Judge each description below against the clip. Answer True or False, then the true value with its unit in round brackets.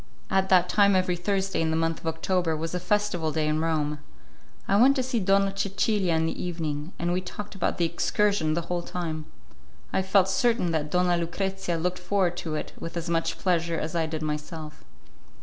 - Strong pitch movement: False (3.0 semitones)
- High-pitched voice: False (175 Hz)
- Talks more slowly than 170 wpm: False (200 wpm)